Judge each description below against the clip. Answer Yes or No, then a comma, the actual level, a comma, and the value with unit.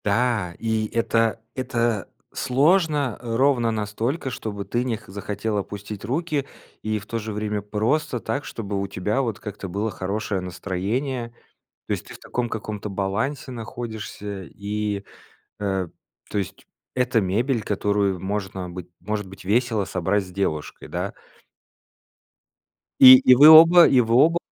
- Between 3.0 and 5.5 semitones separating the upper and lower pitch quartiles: Yes, average, 3.6 semitones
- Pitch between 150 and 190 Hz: No, low, 110 Hz